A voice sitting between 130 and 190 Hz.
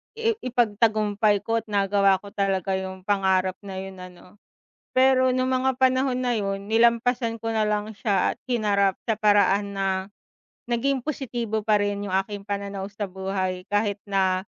No: high, 205 Hz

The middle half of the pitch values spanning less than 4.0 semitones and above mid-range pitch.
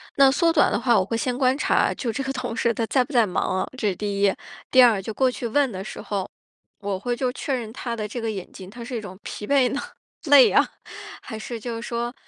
Yes: average, 3.5 semitones; high, 235 Hz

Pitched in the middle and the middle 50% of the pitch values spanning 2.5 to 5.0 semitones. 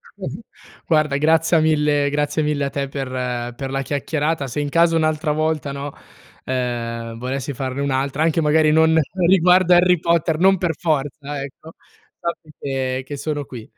Yes: medium, 145 Hz; average, 2.9 semitones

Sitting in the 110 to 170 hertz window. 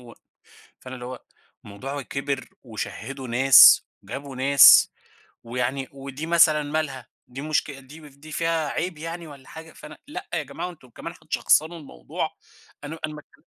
Yes: medium, 140 Hz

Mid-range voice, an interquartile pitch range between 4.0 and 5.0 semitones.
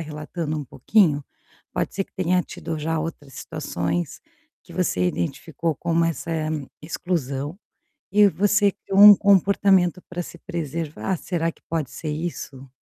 No: medium, 165 Hz; average, 3.6 semitones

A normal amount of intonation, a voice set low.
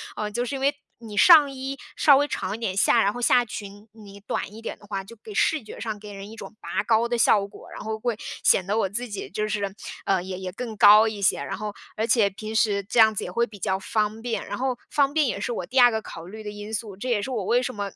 No: average, 3.0 semitones; high, 215 Hz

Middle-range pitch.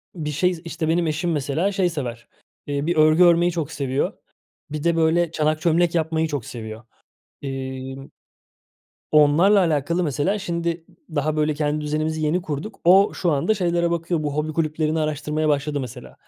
Yes: medium, 155 Hz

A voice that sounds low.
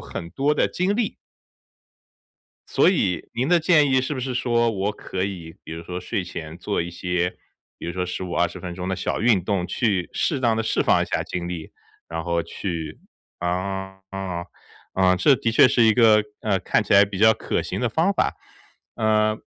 Yes: low, 100 Hz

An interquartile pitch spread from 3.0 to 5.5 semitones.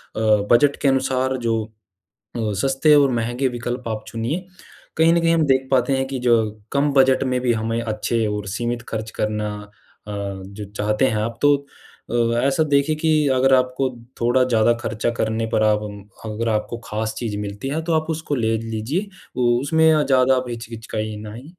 Yes: average, 3.5 semitones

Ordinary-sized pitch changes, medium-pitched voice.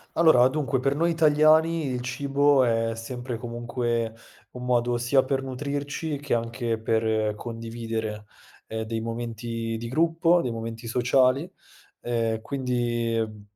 No: average, 3.4 semitones; low, 120 Hz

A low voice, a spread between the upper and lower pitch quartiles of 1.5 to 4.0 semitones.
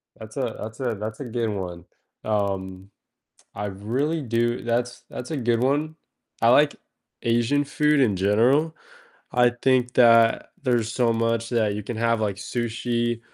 Yes: low, 115 Hz; narrow, 2.6 semitones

